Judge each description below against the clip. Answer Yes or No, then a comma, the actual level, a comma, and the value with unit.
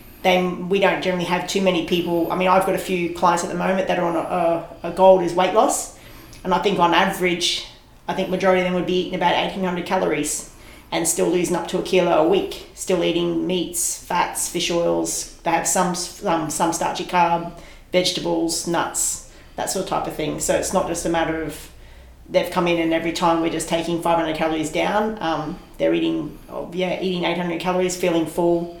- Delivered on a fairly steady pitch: Yes, narrow, 1.6 semitones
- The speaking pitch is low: No, medium, 175 Hz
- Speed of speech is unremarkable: No, fast, 215 wpm